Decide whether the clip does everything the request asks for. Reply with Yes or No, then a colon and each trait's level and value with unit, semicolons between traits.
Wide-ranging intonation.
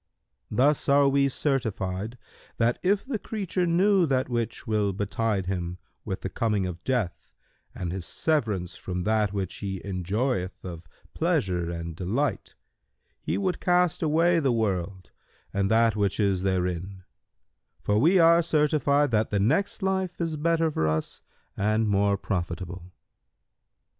Yes: wide, 8.0 semitones